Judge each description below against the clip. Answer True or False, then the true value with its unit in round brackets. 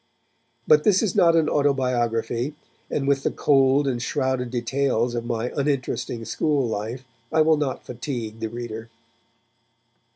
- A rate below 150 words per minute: True (140 wpm)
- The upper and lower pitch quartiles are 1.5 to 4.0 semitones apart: True (3.4 semitones)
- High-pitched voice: False (130 Hz)